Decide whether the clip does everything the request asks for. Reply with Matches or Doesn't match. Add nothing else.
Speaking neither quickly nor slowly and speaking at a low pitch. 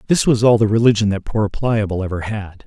Doesn't match